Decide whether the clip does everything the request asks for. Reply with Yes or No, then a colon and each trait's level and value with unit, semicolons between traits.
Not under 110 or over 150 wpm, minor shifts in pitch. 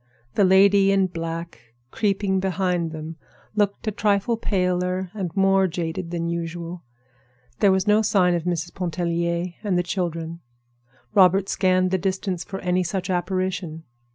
Yes: average, 145 wpm; narrow, 2.2 semitones